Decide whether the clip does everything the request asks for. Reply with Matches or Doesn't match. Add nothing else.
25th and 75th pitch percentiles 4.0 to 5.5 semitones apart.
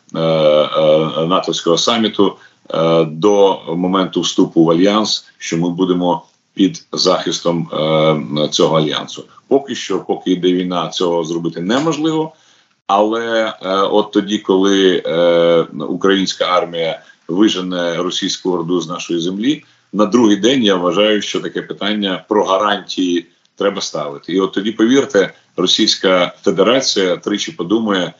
Doesn't match